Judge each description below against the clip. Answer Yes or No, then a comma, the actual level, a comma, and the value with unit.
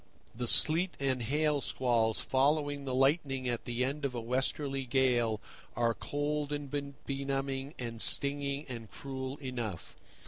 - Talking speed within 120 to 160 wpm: Yes, average, 140 wpm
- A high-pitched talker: No, low, 135 Hz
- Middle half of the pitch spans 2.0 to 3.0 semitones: Yes, narrow, 2.5 semitones